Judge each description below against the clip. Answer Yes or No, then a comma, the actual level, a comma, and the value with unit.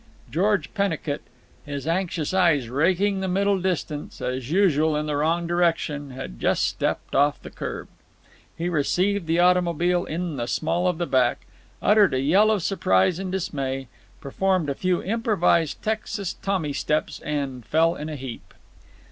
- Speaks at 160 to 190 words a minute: No, average, 150 wpm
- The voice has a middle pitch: Yes, medium, 165 Hz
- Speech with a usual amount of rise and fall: Yes, average, 4.4 semitones